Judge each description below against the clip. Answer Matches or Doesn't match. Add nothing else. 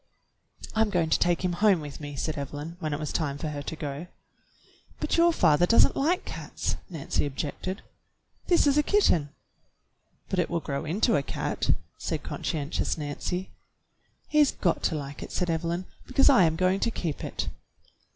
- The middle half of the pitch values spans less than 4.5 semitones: Doesn't match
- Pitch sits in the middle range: Matches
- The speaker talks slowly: Doesn't match